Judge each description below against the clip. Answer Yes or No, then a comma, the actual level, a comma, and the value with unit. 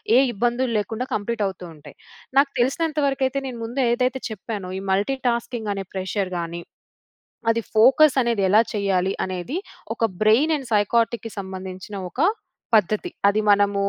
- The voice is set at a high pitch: Yes, high, 220 Hz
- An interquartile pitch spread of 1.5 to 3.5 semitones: No, average, 4.3 semitones